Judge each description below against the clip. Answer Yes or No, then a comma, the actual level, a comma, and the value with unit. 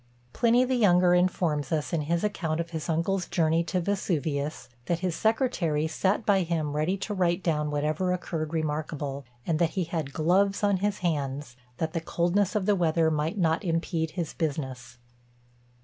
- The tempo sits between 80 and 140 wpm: No, average, 175 wpm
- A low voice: No, medium, 165 Hz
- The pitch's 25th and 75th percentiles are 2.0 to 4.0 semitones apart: Yes, average, 3.2 semitones